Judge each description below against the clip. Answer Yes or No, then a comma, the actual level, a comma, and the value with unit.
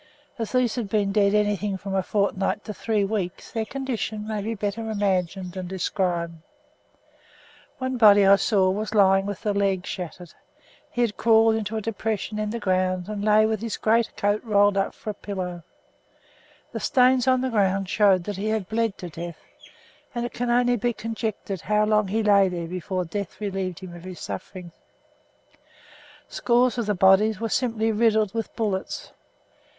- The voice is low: No, high, 205 Hz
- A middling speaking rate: Yes, average, 180 wpm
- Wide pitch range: No, narrow, 2.6 semitones